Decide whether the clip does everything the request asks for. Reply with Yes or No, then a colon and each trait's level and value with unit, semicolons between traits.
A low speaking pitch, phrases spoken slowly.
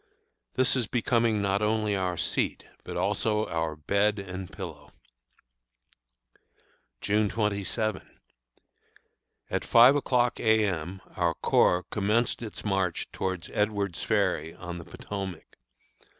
Yes: low, 100 Hz; slow, 115 wpm